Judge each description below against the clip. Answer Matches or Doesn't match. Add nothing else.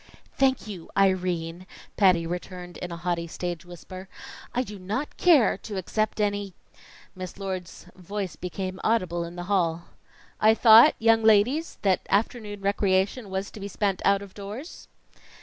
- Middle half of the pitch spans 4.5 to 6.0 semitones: Doesn't match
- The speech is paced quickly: Doesn't match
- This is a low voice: Doesn't match